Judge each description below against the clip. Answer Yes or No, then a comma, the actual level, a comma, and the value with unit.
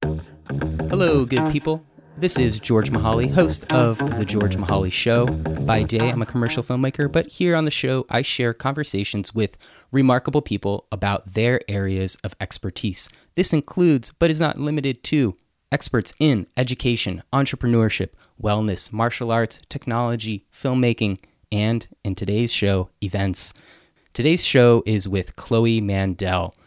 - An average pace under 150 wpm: Yes, average, 140 wpm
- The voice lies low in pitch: Yes, low, 115 Hz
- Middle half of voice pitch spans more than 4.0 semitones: Yes, average, 4.7 semitones